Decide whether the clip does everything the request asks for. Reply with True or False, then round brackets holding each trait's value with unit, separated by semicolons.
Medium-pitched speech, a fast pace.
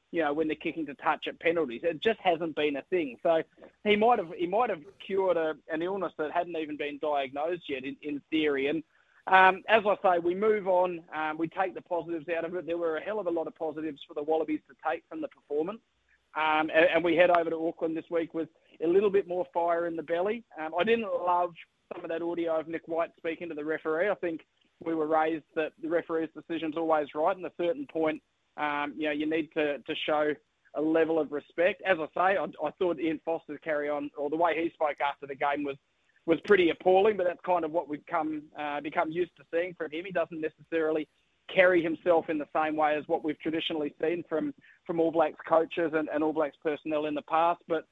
True (160 Hz; 245 wpm)